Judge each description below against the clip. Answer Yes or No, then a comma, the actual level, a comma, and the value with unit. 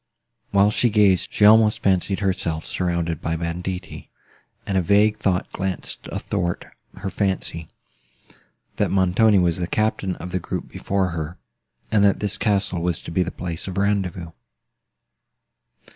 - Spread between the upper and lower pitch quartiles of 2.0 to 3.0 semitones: Yes, average, 2.7 semitones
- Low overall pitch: Yes, very low, 95 Hz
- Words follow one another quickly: No, average, 145 wpm